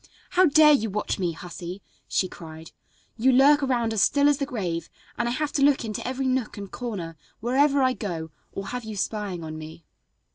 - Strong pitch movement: Yes, wide, 7.0 semitones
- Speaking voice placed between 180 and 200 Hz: No, high, 225 Hz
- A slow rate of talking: No, fast, 205 wpm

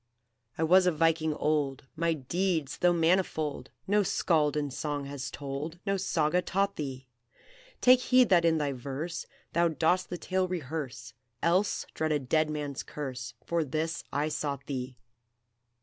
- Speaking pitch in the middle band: Yes, medium, 155 Hz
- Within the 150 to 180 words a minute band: Yes, average, 155 wpm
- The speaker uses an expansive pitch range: No, average, 3.6 semitones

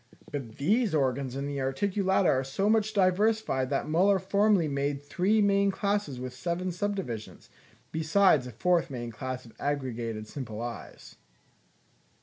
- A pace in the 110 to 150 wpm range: Yes, average, 140 wpm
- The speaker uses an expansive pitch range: Yes, wide, 7.3 semitones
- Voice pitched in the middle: Yes, medium, 155 Hz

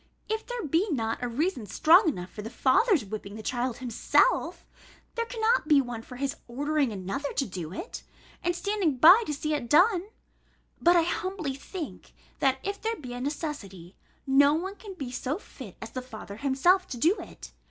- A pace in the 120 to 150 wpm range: No, average, 190 wpm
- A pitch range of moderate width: No, wide, 6.8 semitones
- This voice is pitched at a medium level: No, very high, 285 Hz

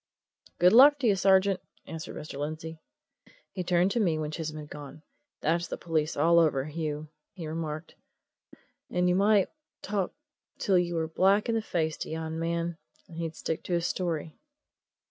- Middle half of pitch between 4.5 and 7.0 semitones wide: No, average, 2.8 semitones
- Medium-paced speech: Yes, average, 175 wpm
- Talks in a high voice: No, medium, 165 Hz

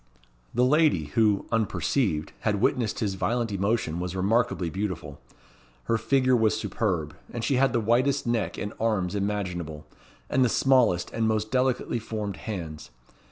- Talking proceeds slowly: No, average, 150 wpm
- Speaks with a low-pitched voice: Yes, low, 110 Hz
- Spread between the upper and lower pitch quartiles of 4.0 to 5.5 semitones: Yes, average, 4.5 semitones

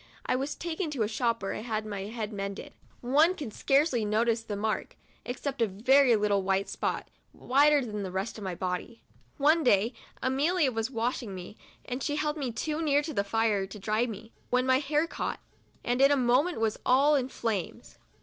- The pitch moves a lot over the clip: No, average, 5.0 semitones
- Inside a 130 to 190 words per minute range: No, average, 200 wpm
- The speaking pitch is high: Yes, high, 240 Hz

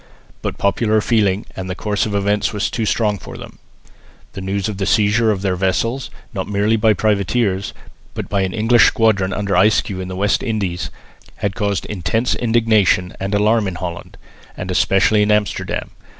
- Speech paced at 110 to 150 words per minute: No, average, 180 wpm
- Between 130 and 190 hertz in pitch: No, low, 105 Hz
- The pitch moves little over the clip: Yes, narrow, 2.2 semitones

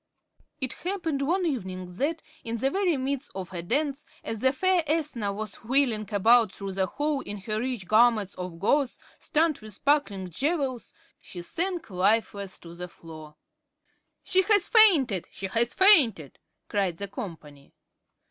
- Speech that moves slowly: No, average, 155 wpm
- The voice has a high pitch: Yes, high, 230 Hz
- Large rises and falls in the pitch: Yes, wide, 7.5 semitones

